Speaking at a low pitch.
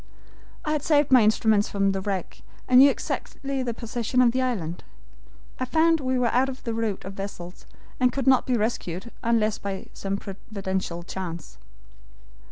No: high, 225 Hz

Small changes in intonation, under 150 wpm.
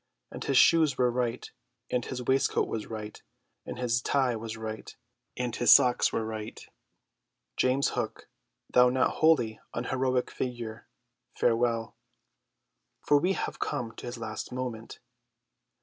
Yes: narrow, 2.2 semitones; slow, 135 wpm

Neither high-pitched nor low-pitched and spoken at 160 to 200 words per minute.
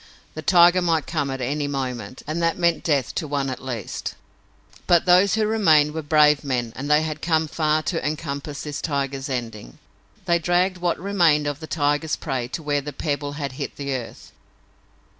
Yes: medium, 150 Hz; average, 190 wpm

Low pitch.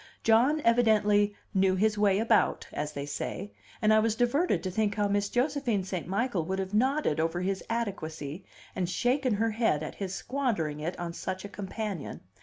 No: high, 205 Hz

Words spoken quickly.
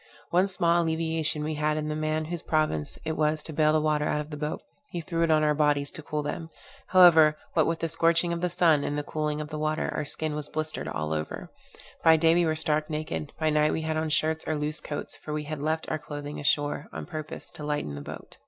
Yes: fast, 245 wpm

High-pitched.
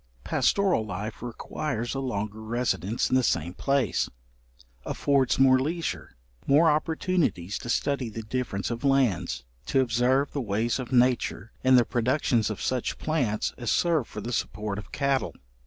No: low, 125 Hz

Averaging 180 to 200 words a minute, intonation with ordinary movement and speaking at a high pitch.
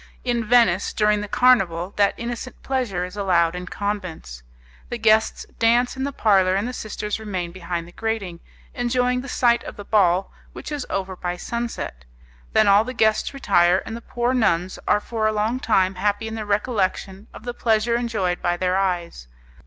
Yes: average, 185 wpm; average, 4.3 semitones; high, 210 Hz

